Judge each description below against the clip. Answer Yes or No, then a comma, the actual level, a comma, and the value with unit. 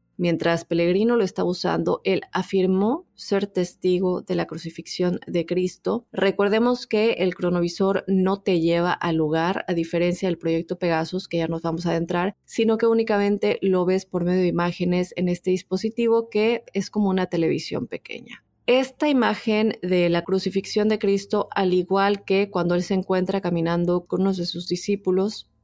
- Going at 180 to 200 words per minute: No, average, 170 wpm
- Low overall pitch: No, medium, 185 Hz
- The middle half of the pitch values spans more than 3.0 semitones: No, narrow, 2.5 semitones